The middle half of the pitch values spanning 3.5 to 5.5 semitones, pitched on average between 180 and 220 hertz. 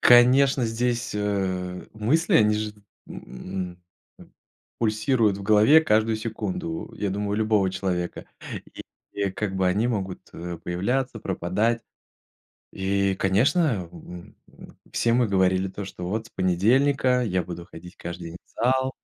No: average, 4.4 semitones; low, 105 Hz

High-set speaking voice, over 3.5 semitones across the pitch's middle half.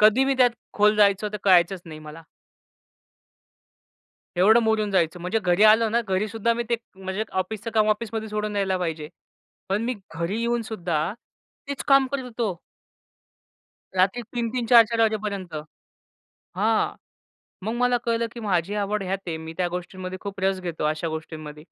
Yes: high, 205 Hz; average, 3.9 semitones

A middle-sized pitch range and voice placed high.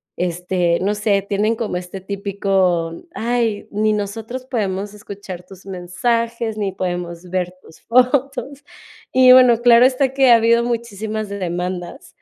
Yes: average, 4.2 semitones; high, 205 Hz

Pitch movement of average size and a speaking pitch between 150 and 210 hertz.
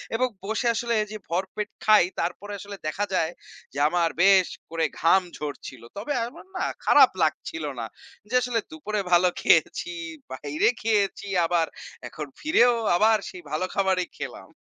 Yes: average, 4.4 semitones; high, 190 Hz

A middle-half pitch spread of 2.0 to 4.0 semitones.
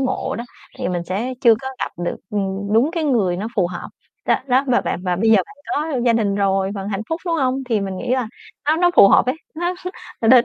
No: average, 5.2 semitones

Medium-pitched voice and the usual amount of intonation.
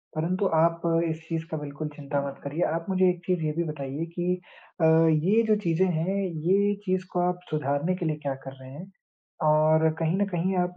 Yes: medium, 165 Hz; average, 3.1 semitones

